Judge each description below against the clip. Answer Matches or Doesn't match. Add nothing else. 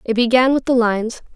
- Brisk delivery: Matches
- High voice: Matches